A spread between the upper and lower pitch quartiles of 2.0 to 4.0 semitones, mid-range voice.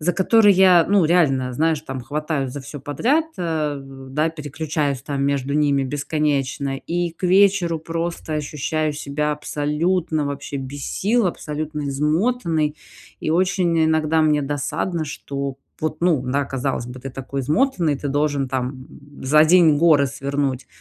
Yes: average, 3.0 semitones; medium, 150 Hz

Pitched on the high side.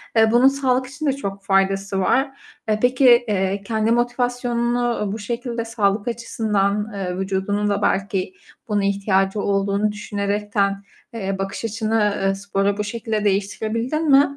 Yes: high, 210 Hz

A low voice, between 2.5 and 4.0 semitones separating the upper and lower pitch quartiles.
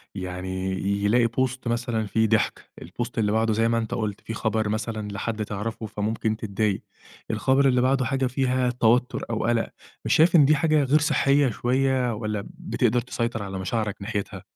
Yes: low, 115 Hz; average, 3.2 semitones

